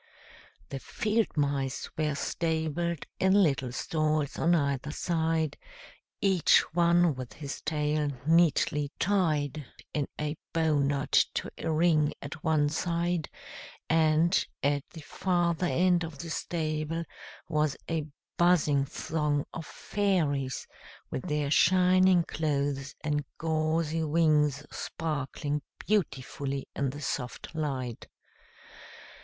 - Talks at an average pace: No, slow, 115 wpm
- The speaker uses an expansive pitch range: No, narrow, 2.6 semitones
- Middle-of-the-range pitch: Yes, medium, 155 Hz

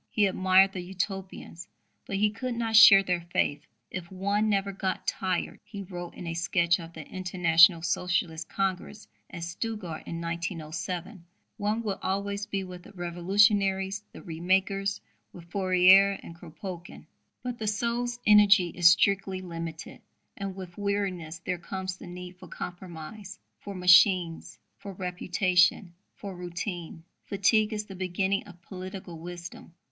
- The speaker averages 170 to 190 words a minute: No, average, 145 wpm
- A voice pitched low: No, medium, 185 Hz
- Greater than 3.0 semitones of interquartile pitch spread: No, narrow, 2.4 semitones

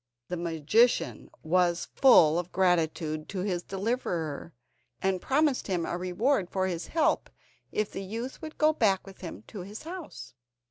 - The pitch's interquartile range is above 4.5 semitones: Yes, average, 5.1 semitones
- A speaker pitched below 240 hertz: Yes, high, 190 Hz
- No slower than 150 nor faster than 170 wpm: Yes, average, 155 wpm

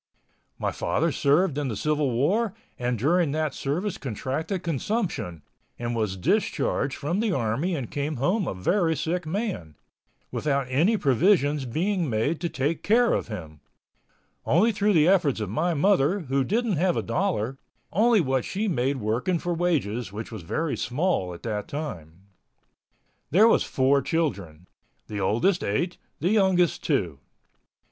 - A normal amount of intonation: No, wide, 7.2 semitones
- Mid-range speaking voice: Yes, medium, 150 Hz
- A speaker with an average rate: Yes, average, 150 wpm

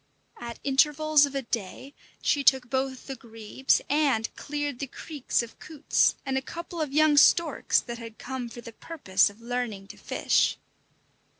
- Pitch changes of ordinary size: Yes, average, 3.8 semitones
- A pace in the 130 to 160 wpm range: No, average, 170 wpm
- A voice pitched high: Yes, very high, 265 Hz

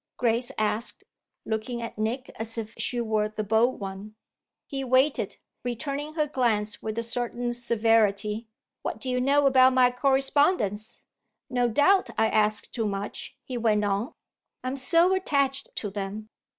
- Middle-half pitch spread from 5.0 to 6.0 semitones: No, average, 3.6 semitones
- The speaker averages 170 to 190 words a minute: No, average, 150 wpm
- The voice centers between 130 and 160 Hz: No, high, 235 Hz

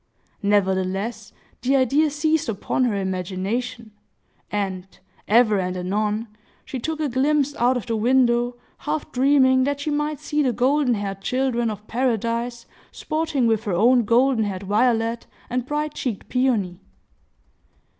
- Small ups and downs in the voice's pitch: No, average, 4.3 semitones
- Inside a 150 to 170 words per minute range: No, average, 140 wpm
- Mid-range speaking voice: No, high, 240 Hz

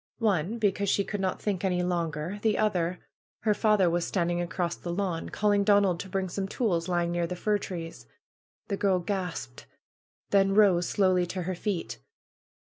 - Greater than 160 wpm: Yes, average, 175 wpm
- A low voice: No, medium, 185 Hz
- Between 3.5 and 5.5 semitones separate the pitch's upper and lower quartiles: No, narrow, 2.6 semitones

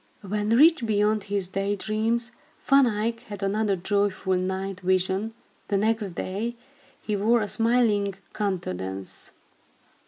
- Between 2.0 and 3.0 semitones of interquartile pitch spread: Yes, average, 2.7 semitones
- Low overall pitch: No, high, 205 Hz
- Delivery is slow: Yes, slow, 125 wpm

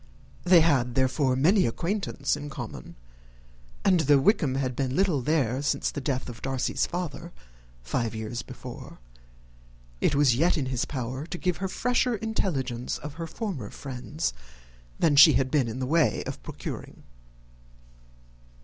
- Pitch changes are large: No, average, 4.6 semitones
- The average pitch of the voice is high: No, medium, 140 Hz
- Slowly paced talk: No, average, 150 wpm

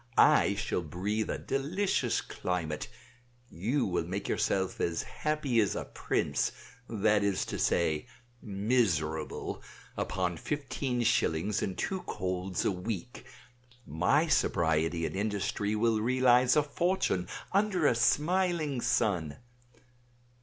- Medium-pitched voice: No, low, 105 Hz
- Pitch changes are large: Yes, wide, 6.8 semitones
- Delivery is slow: Yes, slow, 120 wpm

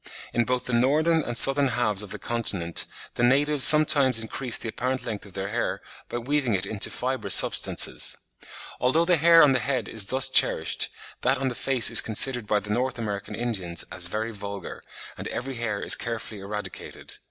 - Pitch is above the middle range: No, low, 120 Hz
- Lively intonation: No, average, 4.1 semitones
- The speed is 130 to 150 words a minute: No, average, 190 wpm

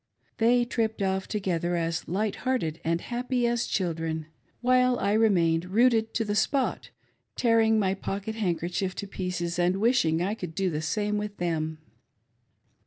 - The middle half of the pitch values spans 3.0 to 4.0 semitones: No, average, 4.7 semitones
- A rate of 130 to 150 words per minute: No, average, 160 wpm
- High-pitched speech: Yes, high, 195 Hz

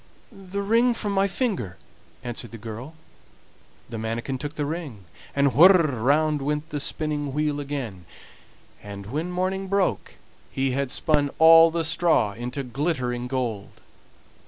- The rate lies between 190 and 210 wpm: No, average, 140 wpm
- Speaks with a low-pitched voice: No, medium, 145 Hz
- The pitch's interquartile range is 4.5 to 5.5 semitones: Yes, average, 5.2 semitones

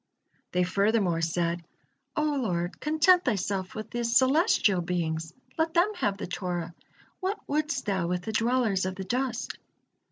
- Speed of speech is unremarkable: Yes, average, 150 wpm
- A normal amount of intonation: No, wide, 6.6 semitones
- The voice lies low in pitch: No, high, 205 Hz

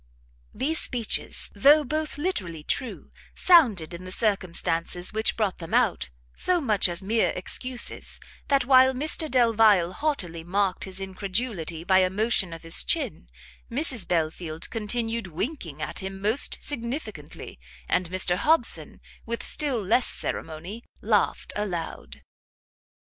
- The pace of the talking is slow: Yes, slow, 130 wpm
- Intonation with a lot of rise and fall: Yes, wide, 6.2 semitones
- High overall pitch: Yes, high, 210 Hz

